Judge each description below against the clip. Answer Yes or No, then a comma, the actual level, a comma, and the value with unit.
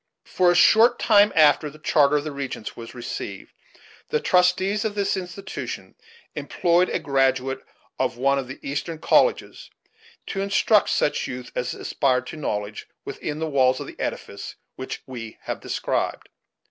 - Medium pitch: Yes, medium, 145 Hz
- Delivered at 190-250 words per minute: No, average, 160 wpm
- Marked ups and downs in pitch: Yes, wide, 5.7 semitones